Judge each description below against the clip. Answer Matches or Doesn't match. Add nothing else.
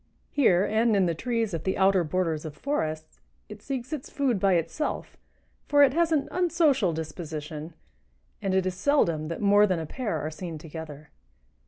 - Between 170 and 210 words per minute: Matches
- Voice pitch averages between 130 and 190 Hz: Matches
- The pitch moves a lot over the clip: Matches